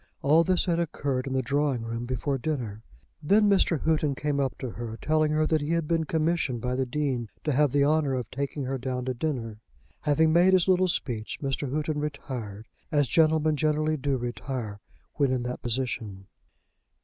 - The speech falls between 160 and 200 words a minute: Yes, average, 185 wpm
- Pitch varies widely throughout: No, average, 3.8 semitones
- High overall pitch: No, medium, 140 Hz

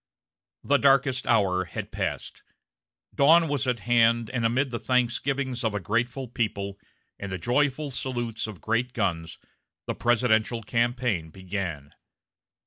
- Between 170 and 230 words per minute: No, slow, 135 wpm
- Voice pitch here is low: Yes, low, 120 Hz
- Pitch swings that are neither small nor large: Yes, average, 3.8 semitones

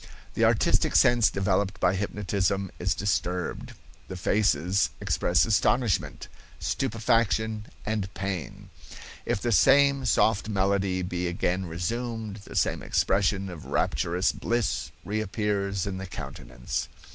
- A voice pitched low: Yes, low, 100 Hz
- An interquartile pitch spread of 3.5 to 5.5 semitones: No, average, 2.8 semitones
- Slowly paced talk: Yes, slow, 115 wpm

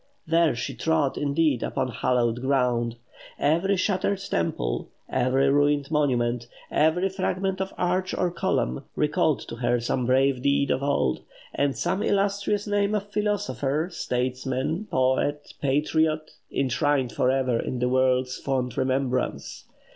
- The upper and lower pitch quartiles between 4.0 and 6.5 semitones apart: Yes, average, 5.1 semitones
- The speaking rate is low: Yes, slow, 130 wpm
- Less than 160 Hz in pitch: Yes, medium, 140 Hz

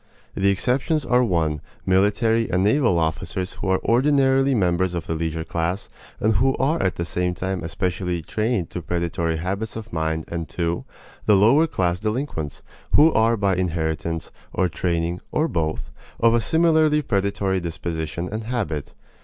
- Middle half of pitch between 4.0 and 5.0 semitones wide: No, wide, 5.4 semitones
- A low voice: Yes, very low, 95 Hz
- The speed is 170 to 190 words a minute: No, average, 160 wpm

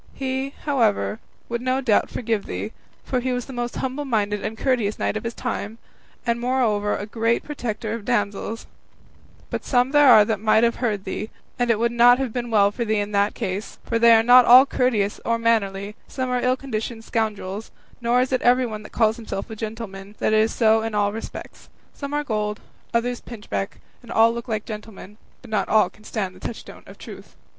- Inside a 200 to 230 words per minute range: Yes, fast, 205 wpm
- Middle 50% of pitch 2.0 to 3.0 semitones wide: Yes, average, 2.7 semitones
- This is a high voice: Yes, high, 230 Hz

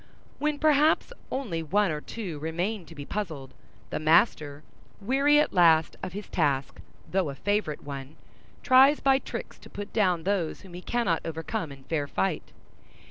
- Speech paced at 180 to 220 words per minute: No, average, 165 wpm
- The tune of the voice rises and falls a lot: Yes, wide, 6.1 semitones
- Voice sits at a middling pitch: Yes, medium, 180 Hz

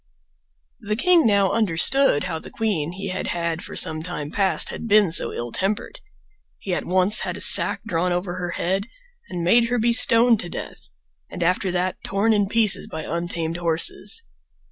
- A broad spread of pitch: No, average, 3.9 semitones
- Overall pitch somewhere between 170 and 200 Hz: Yes, medium, 185 Hz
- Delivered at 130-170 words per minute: No, average, 185 wpm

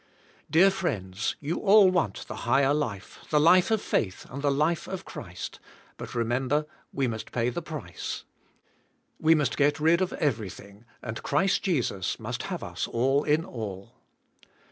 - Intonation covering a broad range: Yes, wide, 6.3 semitones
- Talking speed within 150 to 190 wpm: Yes, average, 160 wpm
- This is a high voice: No, medium, 140 Hz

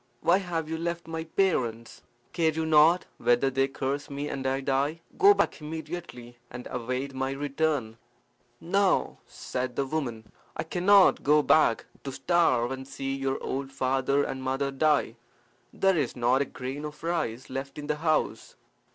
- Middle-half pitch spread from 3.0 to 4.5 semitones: Yes, average, 3.4 semitones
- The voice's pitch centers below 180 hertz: Yes, medium, 140 Hz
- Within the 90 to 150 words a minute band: No, average, 170 wpm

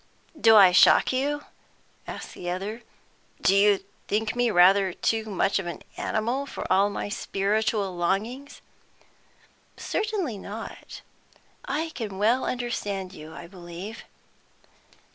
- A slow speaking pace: Yes, slow, 125 wpm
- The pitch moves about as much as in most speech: Yes, average, 3.9 semitones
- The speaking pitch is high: Yes, high, 210 Hz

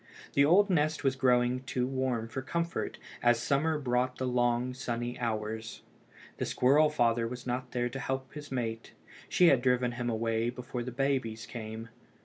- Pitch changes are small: Yes, narrow, 2.1 semitones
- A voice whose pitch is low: Yes, low, 125 Hz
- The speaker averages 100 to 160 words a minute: No, average, 170 wpm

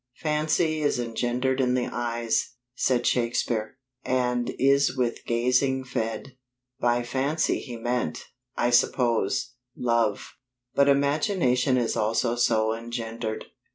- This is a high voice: No, low, 125 Hz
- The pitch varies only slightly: Yes, narrow, 2.1 semitones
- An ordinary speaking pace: No, slow, 115 wpm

